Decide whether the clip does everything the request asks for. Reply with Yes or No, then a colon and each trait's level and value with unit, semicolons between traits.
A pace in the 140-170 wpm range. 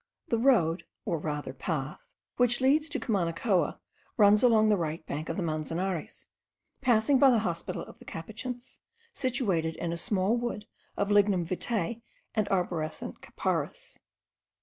Yes: average, 145 wpm